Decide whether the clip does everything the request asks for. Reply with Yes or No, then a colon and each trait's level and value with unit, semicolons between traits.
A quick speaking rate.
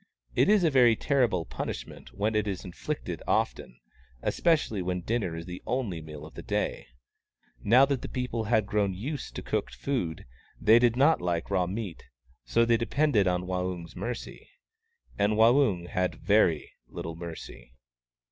No: average, 160 wpm